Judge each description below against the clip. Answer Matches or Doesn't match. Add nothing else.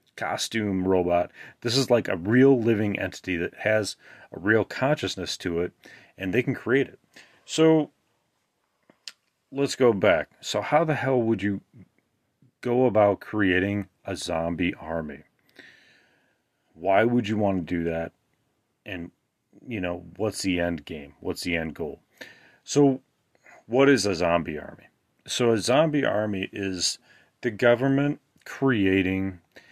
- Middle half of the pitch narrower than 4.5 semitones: Doesn't match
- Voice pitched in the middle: Doesn't match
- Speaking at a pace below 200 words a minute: Matches